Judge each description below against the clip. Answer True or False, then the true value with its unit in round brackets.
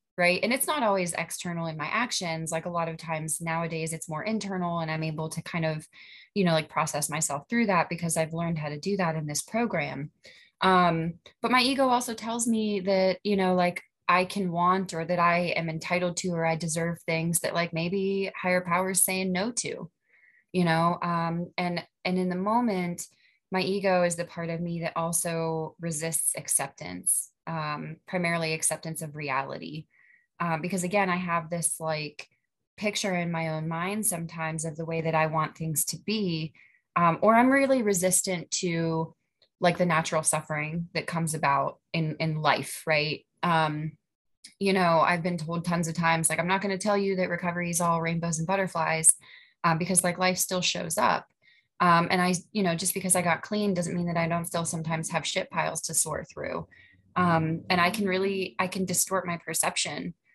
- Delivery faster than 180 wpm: True (200 wpm)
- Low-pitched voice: False (170 Hz)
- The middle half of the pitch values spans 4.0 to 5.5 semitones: False (2.4 semitones)